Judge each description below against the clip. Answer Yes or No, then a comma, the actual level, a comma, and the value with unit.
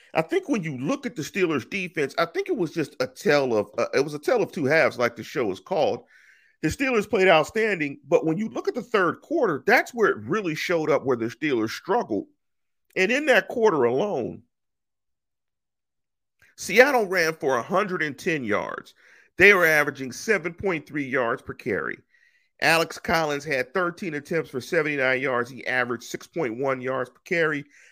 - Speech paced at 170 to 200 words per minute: Yes, average, 180 wpm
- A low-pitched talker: No, medium, 175 Hz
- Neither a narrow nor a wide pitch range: No, wide, 8.0 semitones